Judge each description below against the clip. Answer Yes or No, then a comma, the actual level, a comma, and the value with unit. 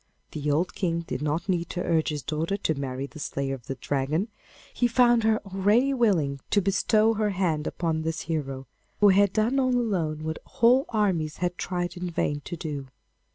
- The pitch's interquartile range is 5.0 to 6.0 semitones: Yes, wide, 5.4 semitones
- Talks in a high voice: No, medium, 175 Hz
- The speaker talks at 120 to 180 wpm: No, average, 195 wpm